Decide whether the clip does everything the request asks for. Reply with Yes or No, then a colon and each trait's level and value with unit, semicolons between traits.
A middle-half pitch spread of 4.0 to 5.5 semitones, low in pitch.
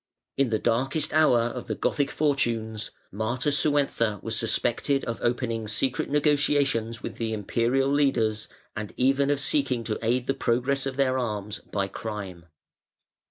No: average, 3.6 semitones; low, 120 Hz